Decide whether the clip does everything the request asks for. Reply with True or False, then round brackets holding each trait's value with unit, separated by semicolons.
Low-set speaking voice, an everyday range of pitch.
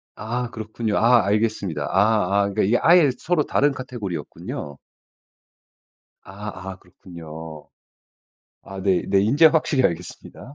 True (105 Hz; 5.0 semitones)